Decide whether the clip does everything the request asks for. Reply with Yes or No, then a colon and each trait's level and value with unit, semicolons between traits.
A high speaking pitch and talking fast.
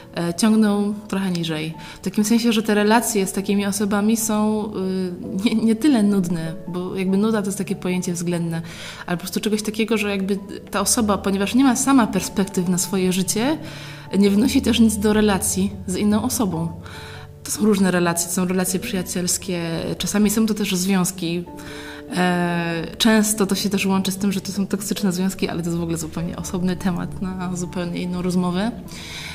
Yes: high, 195 Hz; fast, 180 wpm